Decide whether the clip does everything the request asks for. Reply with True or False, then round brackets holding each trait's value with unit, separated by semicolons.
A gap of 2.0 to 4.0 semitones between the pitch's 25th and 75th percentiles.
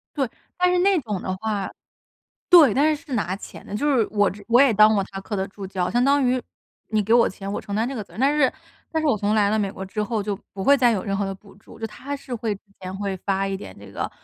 False (4.8 semitones)